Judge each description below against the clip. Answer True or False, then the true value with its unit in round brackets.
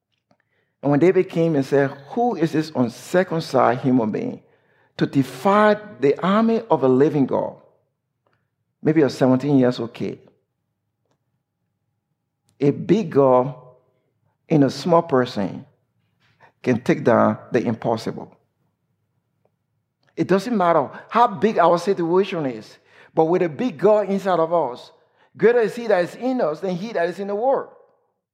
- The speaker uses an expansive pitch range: True (6.7 semitones)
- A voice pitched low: False (155 Hz)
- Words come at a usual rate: True (150 wpm)